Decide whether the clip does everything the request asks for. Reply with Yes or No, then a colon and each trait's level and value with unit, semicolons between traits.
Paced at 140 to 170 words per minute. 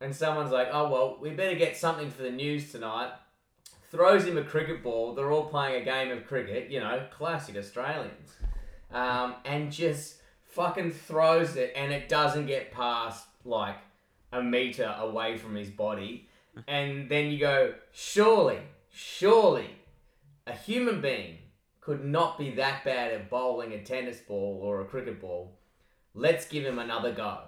Yes: average, 165 wpm